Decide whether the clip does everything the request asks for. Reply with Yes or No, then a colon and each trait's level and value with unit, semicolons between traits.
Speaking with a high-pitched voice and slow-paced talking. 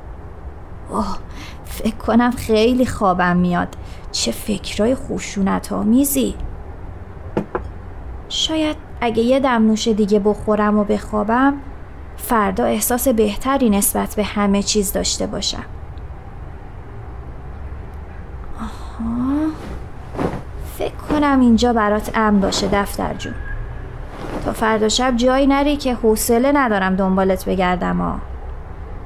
Yes: high, 210 Hz; slow, 100 wpm